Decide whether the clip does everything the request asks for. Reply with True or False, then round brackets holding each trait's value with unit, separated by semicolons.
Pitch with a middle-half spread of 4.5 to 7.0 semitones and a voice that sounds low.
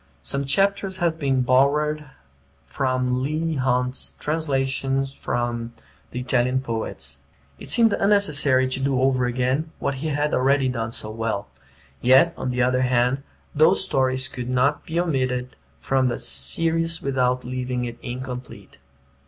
False (2.7 semitones; 130 Hz)